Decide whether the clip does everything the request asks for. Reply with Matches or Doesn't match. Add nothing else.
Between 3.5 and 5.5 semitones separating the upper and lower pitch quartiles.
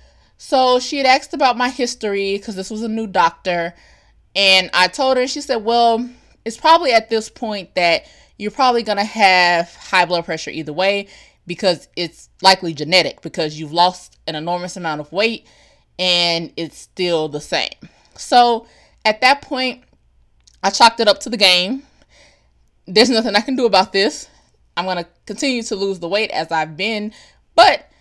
Matches